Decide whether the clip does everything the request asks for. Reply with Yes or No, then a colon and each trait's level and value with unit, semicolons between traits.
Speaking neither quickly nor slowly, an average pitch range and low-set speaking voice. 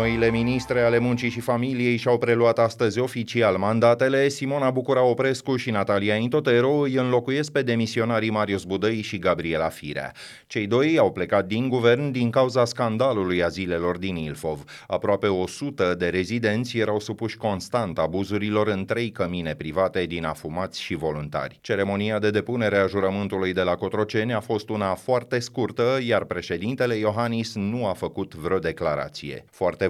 Yes: average, 155 wpm; average, 4.2 semitones; low, 110 Hz